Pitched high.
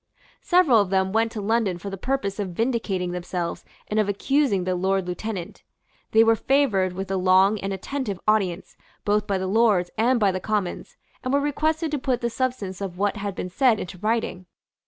Yes: high, 205 Hz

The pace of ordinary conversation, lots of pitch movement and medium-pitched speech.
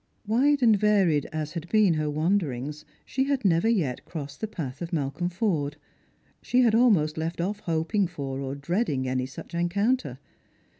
Yes: average, 165 wpm; wide, 6.2 semitones; medium, 170 Hz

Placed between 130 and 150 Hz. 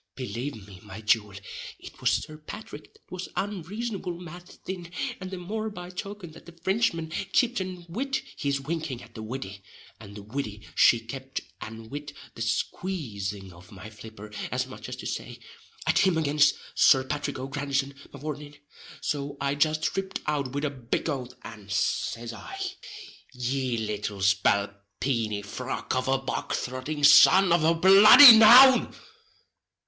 Yes: medium, 140 Hz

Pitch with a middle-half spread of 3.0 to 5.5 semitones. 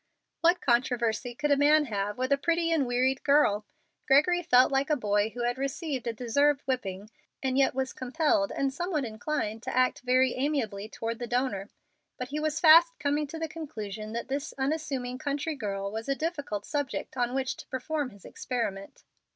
Yes: average, 4.0 semitones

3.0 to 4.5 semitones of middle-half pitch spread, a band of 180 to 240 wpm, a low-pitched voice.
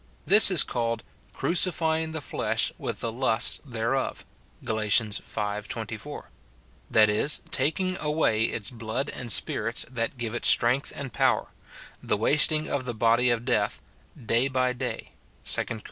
No: average, 4.1 semitones; average, 155 wpm; low, 120 Hz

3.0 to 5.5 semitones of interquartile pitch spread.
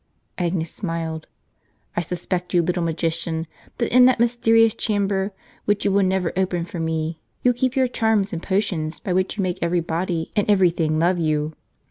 Yes: average, 3.6 semitones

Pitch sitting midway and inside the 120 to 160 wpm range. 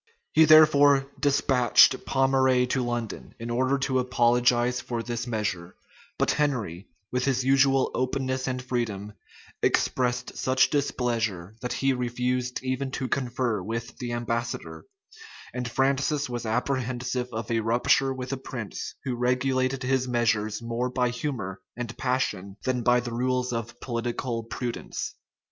No: low, 125 Hz; average, 140 wpm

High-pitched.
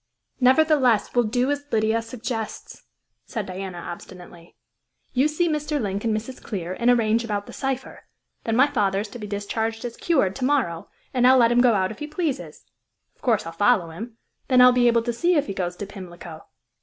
Yes: high, 230 Hz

